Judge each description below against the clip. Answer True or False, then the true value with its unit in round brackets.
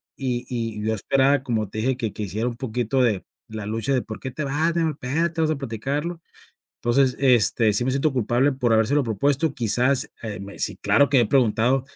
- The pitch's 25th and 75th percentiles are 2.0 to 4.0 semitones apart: True (3.7 semitones)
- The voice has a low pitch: True (125 Hz)